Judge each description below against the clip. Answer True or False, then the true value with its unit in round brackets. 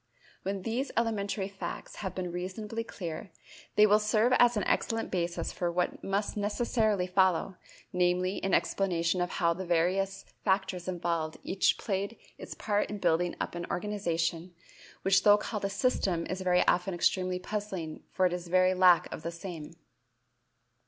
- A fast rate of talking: False (160 wpm)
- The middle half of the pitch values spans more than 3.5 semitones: False (2.6 semitones)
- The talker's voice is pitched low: False (185 Hz)